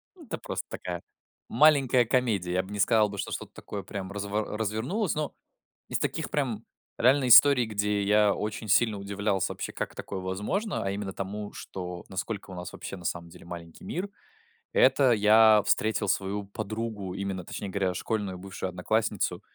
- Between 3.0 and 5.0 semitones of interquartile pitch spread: No, narrow, 2.6 semitones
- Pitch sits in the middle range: No, low, 105 Hz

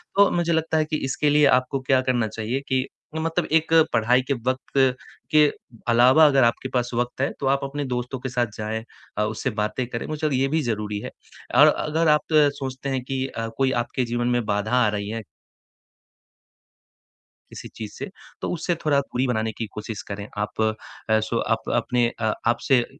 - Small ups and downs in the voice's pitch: No, average, 3.6 semitones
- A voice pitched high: No, low, 125 Hz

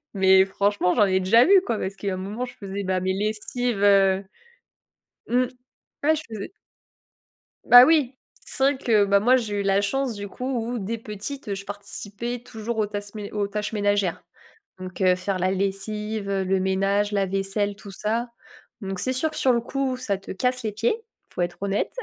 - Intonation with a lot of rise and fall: No, average, 3.4 semitones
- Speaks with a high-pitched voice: Yes, high, 205 Hz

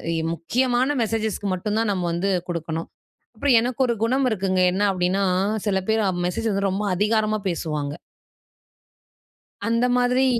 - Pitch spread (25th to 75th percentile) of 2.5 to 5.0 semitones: Yes, average, 3.9 semitones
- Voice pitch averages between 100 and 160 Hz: No, high, 210 Hz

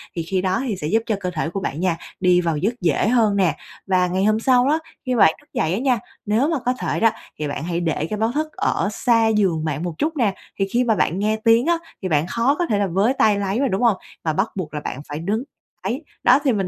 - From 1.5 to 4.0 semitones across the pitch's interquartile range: No, average, 5.0 semitones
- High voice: Yes, high, 200 Hz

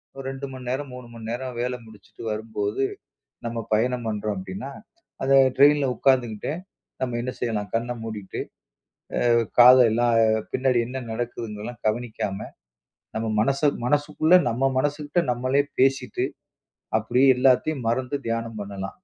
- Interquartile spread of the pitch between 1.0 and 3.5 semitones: Yes, average, 3.0 semitones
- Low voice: Yes, low, 120 Hz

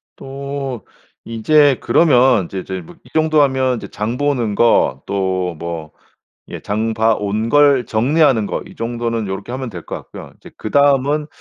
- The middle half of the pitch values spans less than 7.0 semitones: Yes, average, 5.2 semitones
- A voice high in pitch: No, low, 120 Hz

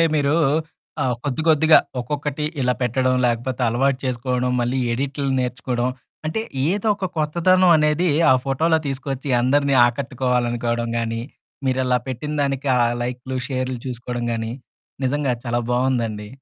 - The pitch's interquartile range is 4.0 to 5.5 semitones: No, average, 2.9 semitones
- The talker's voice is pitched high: No, low, 130 Hz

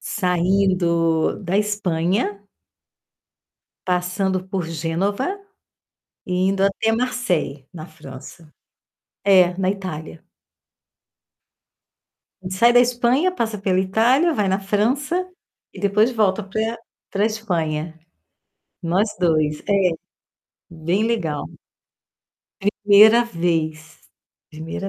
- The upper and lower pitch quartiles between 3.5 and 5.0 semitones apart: Yes, average, 4.4 semitones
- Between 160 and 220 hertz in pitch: Yes, high, 190 Hz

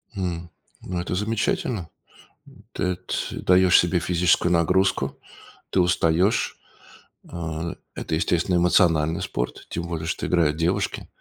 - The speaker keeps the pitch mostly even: Yes, narrow, 1.7 semitones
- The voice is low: Yes, very low, 85 Hz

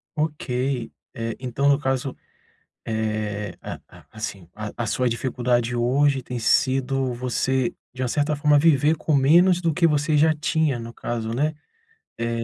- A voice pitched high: No, low, 130 Hz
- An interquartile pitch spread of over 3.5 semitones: Yes, average, 3.9 semitones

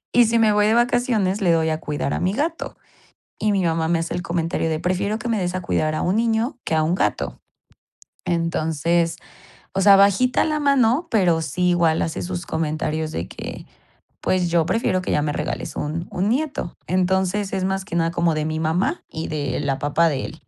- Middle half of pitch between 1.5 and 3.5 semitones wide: No, average, 4.4 semitones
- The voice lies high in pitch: No, medium, 180 Hz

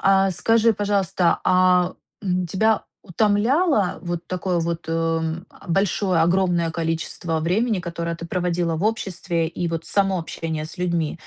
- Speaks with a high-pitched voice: No, medium, 180 Hz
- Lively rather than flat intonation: No, narrow, 2.6 semitones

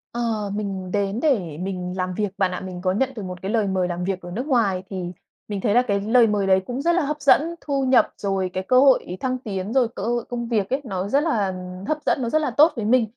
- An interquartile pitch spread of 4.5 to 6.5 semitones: Yes, average, 5.2 semitones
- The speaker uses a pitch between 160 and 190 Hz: No, high, 210 Hz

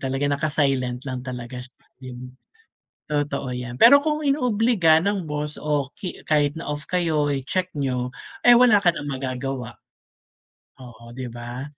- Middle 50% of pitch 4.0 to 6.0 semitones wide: Yes, average, 4.6 semitones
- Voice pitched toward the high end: No, medium, 145 Hz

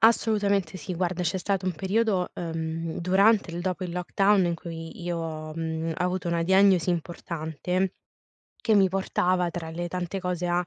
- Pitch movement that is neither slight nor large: No, narrow, 2.1 semitones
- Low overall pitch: No, medium, 180 Hz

